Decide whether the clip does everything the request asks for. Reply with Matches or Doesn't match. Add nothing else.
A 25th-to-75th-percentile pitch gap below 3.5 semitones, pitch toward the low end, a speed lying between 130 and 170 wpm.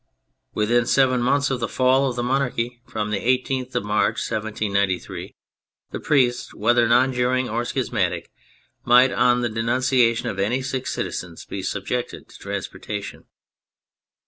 Matches